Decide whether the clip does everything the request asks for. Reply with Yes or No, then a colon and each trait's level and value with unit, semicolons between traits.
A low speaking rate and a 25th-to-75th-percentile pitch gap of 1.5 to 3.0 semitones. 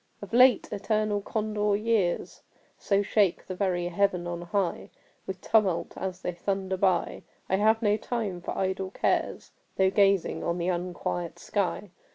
No: average, 155 wpm; narrow, 2.5 semitones